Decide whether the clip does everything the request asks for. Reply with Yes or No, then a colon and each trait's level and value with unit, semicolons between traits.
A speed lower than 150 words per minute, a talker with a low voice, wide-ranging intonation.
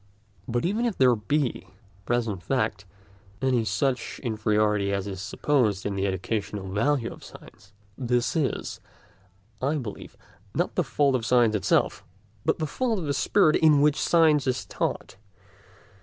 No: average, 155 wpm; low, 120 Hz; wide, 5.9 semitones